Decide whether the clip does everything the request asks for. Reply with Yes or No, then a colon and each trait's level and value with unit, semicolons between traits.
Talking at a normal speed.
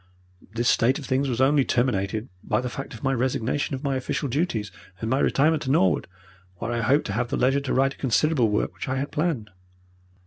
No: fast, 220 wpm